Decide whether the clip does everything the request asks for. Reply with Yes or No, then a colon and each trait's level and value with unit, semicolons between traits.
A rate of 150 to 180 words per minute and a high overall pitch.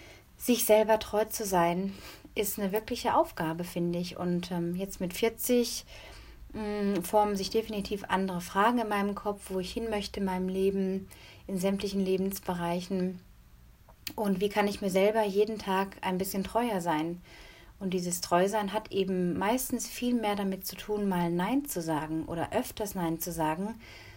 Yes: average, 165 wpm; high, 195 Hz